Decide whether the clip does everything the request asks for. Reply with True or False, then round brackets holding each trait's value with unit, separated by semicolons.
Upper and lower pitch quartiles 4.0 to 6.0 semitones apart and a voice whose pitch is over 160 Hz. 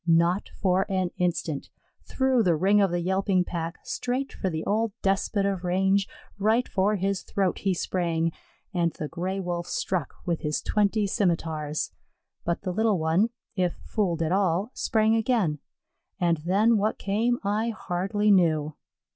False (3.3 semitones; 190 Hz)